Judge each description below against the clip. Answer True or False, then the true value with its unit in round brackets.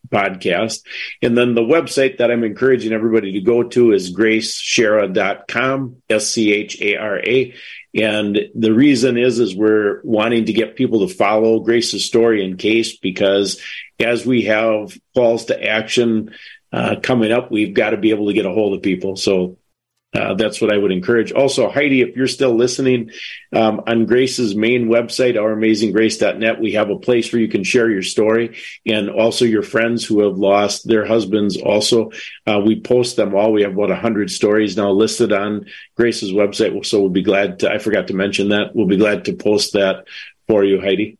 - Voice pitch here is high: False (110 Hz)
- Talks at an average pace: True (190 wpm)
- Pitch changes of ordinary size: False (2.3 semitones)